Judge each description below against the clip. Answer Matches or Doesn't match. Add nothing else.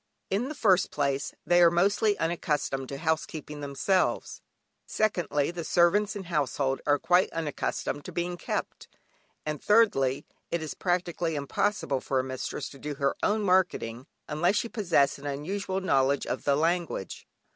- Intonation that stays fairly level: Doesn't match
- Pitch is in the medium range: Matches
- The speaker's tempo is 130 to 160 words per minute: Matches